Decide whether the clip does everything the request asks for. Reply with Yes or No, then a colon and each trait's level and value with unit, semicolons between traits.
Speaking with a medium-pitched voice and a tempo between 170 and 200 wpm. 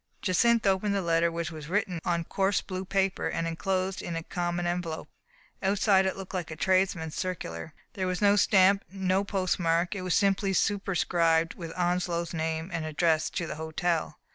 Yes: medium, 180 Hz; average, 175 wpm